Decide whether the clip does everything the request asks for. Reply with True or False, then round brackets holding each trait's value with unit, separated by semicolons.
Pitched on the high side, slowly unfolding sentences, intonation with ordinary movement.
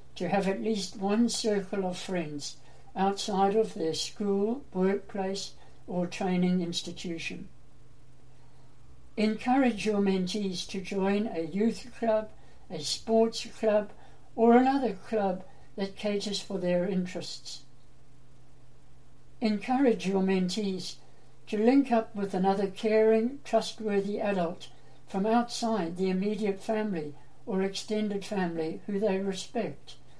True (195 Hz; 115 wpm; 3.3 semitones)